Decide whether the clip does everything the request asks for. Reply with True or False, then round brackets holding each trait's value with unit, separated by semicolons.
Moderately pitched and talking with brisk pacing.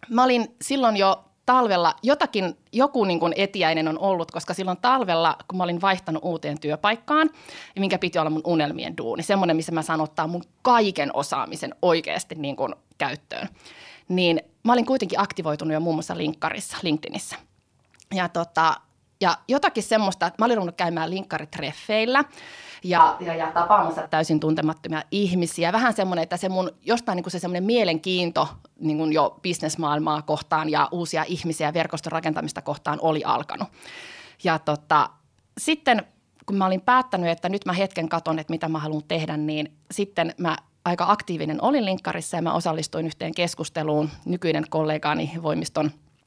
True (170 Hz; 160 wpm)